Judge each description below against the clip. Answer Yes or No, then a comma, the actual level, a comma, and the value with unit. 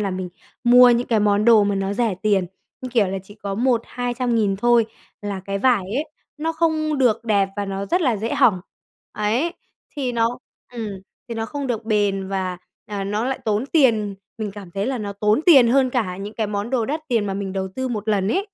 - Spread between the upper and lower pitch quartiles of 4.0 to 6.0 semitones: No, average, 3.6 semitones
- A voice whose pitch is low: No, high, 220 Hz